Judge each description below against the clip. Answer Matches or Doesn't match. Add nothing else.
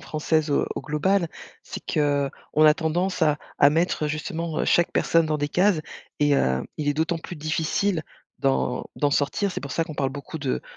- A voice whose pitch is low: Doesn't match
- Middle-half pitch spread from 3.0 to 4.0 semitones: Doesn't match